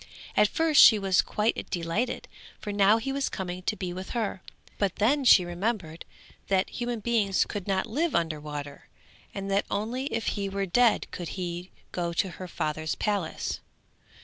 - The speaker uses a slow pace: No, average, 175 wpm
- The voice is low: No, high, 195 Hz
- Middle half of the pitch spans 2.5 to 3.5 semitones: No, average, 4.1 semitones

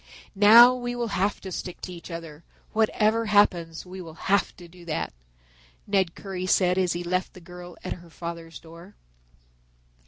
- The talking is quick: No, average, 175 wpm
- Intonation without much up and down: No, average, 3.1 semitones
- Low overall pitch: No, medium, 180 Hz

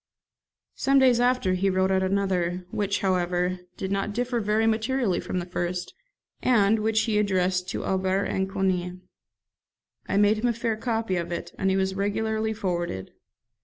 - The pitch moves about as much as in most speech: Yes, average, 3.1 semitones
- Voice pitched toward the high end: Yes, high, 195 Hz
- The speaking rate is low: No, average, 165 wpm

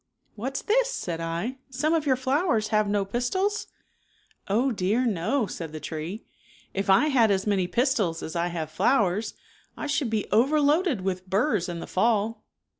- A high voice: Yes, high, 215 Hz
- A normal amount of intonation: No, wide, 6.3 semitones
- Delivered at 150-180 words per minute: No, average, 190 wpm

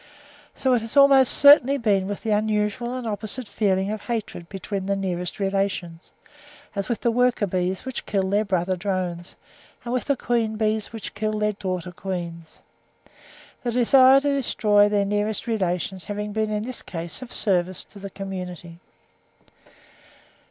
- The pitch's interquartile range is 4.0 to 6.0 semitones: No, average, 3.4 semitones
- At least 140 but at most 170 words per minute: Yes, average, 160 wpm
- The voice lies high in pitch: Yes, high, 205 Hz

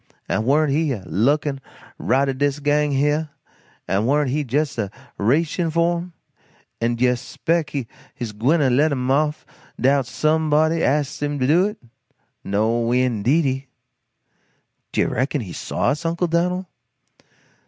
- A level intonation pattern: No, average, 3.7 semitones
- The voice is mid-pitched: Yes, medium, 145 Hz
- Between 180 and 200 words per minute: No, average, 150 wpm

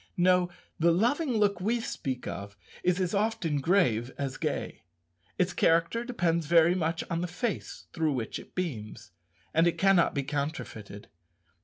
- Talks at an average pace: Yes, average, 155 wpm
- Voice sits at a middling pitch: Yes, medium, 170 Hz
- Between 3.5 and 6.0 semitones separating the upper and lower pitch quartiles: Yes, average, 4.8 semitones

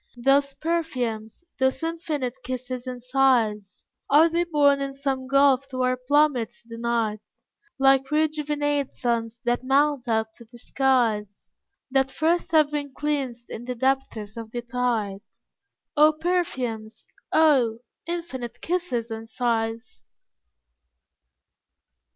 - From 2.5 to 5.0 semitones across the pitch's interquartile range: Yes, average, 3.7 semitones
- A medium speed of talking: No, slow, 120 wpm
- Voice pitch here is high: Yes, very high, 260 Hz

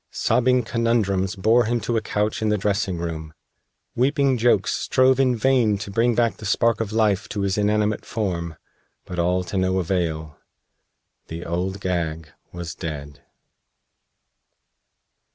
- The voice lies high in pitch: No, low, 100 Hz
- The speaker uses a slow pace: No, average, 145 wpm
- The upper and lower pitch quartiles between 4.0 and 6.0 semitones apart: Yes, average, 4.7 semitones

